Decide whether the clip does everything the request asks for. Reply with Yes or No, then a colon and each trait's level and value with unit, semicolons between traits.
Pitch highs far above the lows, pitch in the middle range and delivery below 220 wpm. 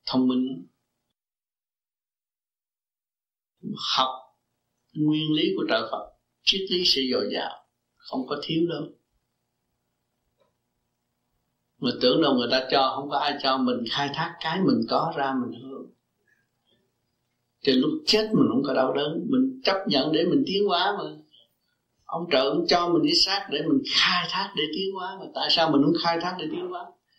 Yes: wide, 6.9 semitones; medium, 160 Hz; average, 170 wpm